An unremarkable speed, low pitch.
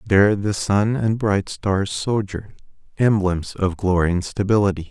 Yes: average, 145 wpm; low, 100 Hz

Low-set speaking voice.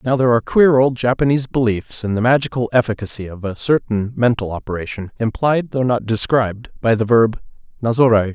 Yes: low, 115 Hz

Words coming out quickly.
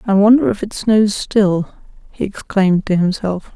No: average, 170 wpm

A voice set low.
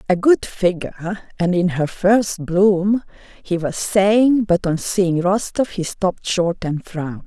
No: high, 190 Hz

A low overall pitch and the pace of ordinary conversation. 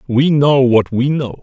No: low, 130 Hz; fast, 210 wpm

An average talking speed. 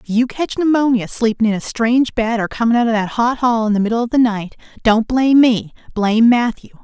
No: fast, 235 wpm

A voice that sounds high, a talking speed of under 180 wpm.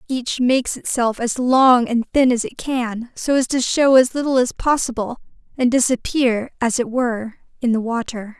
No: high, 245 Hz; average, 185 wpm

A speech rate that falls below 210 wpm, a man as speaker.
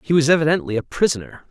Yes: average, 200 wpm; male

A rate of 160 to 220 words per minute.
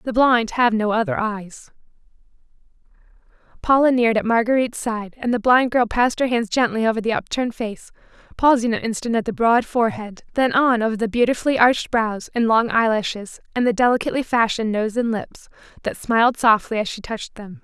Yes: average, 185 wpm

